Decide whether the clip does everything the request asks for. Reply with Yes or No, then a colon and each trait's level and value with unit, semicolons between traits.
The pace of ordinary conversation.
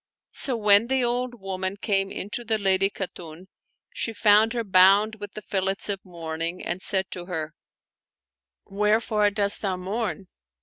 Yes: average, 165 wpm